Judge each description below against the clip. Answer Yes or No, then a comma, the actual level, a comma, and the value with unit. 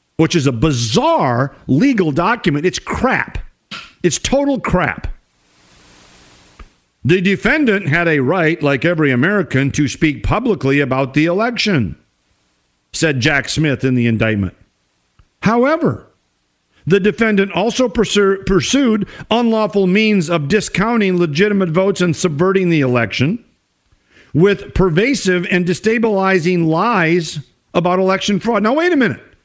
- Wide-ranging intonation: Yes, wide, 6.8 semitones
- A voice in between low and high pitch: Yes, medium, 175 Hz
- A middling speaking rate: No, slow, 120 wpm